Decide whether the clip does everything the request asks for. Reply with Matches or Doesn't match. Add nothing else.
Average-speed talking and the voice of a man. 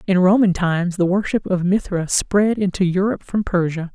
Doesn't match